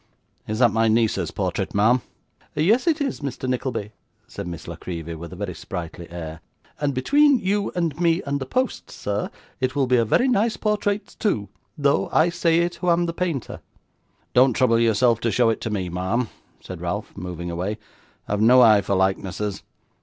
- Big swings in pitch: Yes, wide, 8.9 semitones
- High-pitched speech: No, low, 120 Hz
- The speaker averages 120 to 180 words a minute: No, average, 190 wpm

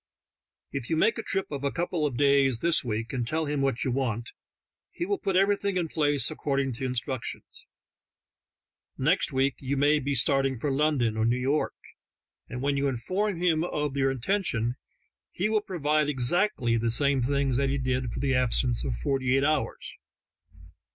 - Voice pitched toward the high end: No, medium, 140 Hz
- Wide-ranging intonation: No, average, 3.5 semitones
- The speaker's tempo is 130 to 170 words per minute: No, average, 180 wpm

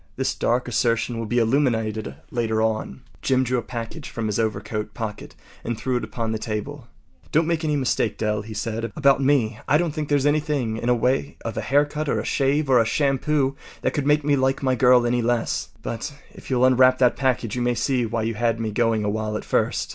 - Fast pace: Yes, fast, 225 wpm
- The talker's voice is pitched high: No, low, 120 Hz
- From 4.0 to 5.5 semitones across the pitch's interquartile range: No, average, 3.5 semitones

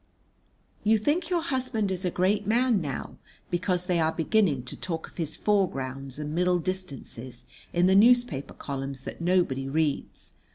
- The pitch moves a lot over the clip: Yes, wide, 6.6 semitones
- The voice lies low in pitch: No, medium, 180 Hz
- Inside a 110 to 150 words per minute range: No, average, 160 wpm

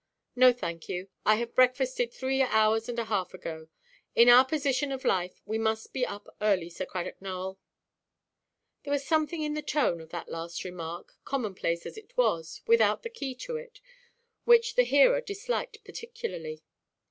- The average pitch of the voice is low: No, high, 245 Hz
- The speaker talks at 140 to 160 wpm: No, average, 170 wpm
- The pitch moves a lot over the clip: Yes, wide, 8.3 semitones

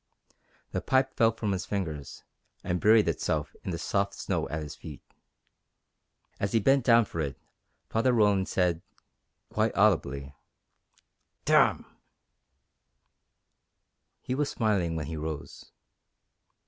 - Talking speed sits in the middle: No, slow, 120 wpm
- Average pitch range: No, wide, 6.1 semitones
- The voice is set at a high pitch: No, very low, 95 Hz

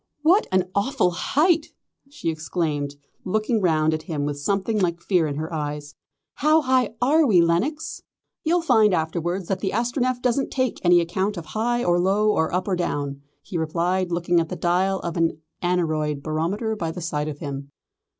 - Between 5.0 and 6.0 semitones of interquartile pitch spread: Yes, wide, 5.4 semitones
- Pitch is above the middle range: No, medium, 175 Hz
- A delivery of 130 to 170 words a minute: No, average, 180 wpm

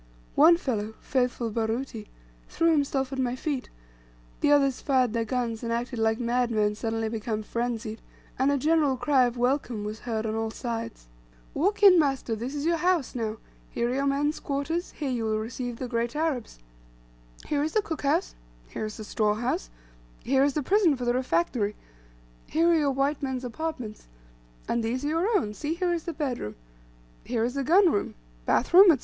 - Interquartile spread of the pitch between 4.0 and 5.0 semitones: Yes, average, 4.5 semitones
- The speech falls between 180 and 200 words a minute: Yes, average, 190 wpm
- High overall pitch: Yes, very high, 255 Hz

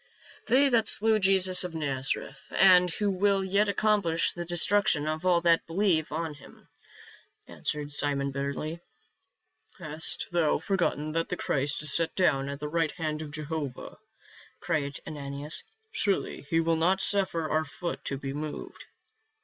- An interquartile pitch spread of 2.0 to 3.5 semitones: No, average, 3.9 semitones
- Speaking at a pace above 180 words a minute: No, average, 155 wpm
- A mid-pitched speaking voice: Yes, medium, 165 Hz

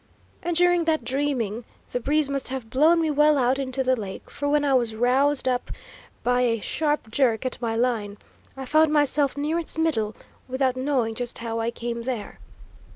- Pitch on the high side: Yes, very high, 260 Hz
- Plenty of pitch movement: No, average, 3.7 semitones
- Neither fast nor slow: Yes, average, 190 wpm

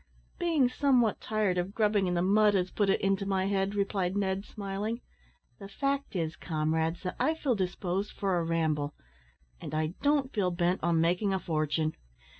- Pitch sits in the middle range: No, high, 195 Hz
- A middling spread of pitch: Yes, average, 3.4 semitones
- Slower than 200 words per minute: Yes, average, 180 wpm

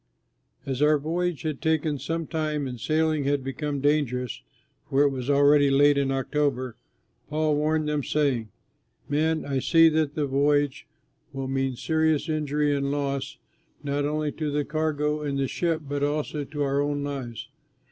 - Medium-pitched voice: Yes, medium, 145 Hz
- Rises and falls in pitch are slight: Yes, narrow, 1.8 semitones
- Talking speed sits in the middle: Yes, average, 165 wpm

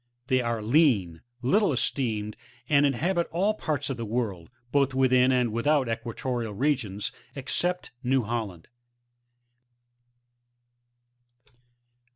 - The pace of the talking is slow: Yes, slow, 110 wpm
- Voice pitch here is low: Yes, low, 125 Hz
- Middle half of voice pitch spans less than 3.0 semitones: No, average, 4.0 semitones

